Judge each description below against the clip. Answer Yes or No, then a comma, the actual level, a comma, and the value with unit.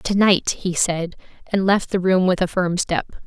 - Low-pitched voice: No, medium, 185 Hz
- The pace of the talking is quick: Yes, fast, 220 wpm